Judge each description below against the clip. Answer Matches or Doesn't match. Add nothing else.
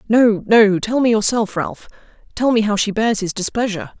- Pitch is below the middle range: Doesn't match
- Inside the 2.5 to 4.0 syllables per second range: Doesn't match